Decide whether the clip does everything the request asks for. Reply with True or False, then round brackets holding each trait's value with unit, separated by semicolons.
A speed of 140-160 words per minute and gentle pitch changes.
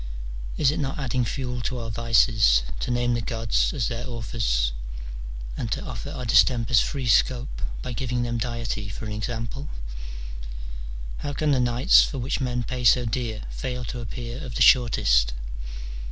False (170 wpm; 1.9 semitones)